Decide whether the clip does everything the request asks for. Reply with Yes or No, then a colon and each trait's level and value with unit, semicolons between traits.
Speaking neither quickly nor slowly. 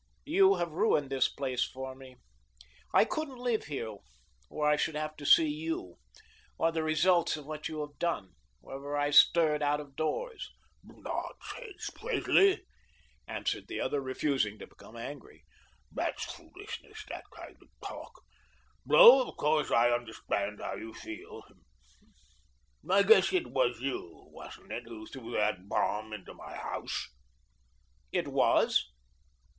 Yes: average, 145 wpm